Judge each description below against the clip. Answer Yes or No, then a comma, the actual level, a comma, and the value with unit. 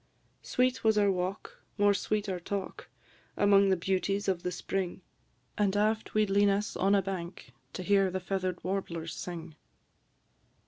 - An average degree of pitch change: No, narrow, 1.9 semitones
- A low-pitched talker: No, high, 195 Hz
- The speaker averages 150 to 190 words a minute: Yes, average, 165 wpm